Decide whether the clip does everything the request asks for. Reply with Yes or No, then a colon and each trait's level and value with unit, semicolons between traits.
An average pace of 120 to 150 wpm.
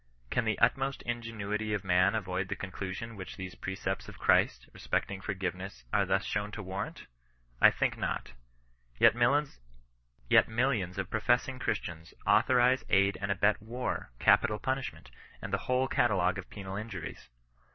Yes: average, 145 wpm